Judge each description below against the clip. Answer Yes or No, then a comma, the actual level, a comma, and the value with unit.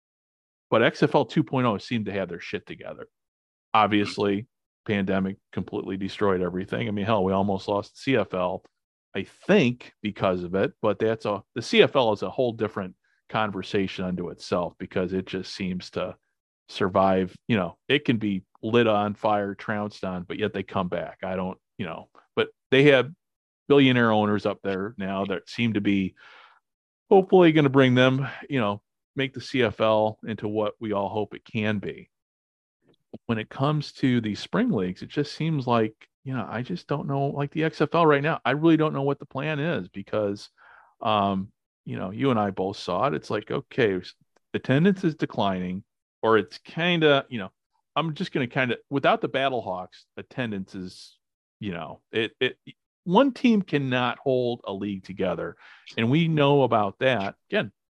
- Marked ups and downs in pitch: Yes, wide, 5.8 semitones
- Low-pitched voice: Yes, low, 110 Hz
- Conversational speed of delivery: Yes, average, 180 wpm